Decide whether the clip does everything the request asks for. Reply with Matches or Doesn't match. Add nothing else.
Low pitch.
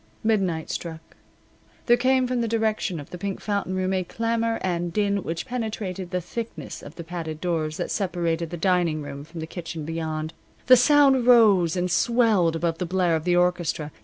Doesn't match